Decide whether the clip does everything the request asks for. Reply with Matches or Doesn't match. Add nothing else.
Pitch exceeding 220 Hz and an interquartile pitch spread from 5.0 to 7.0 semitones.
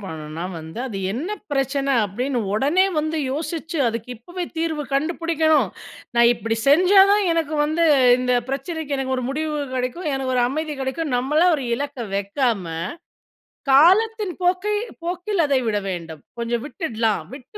Matches